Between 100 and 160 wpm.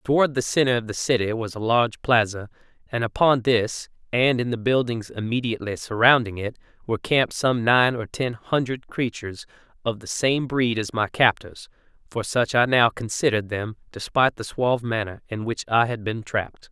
No: average, 185 wpm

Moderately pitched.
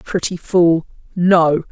Yes: medium, 170 Hz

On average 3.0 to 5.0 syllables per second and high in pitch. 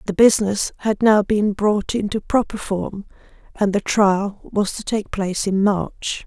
Yes: 4.2 syllables/s; high, 205 Hz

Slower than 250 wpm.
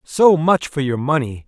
Yes: fast, 205 wpm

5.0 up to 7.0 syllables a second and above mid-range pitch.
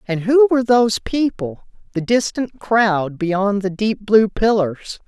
No: 3.9 syllables/s; high, 210 Hz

